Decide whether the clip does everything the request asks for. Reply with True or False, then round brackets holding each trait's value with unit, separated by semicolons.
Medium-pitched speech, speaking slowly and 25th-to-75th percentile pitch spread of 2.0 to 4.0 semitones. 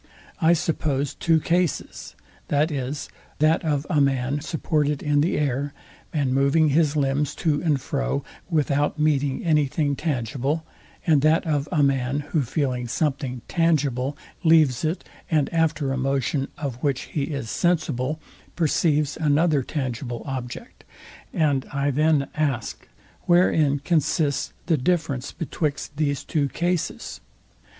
True (145 Hz; 130 wpm; 2.5 semitones)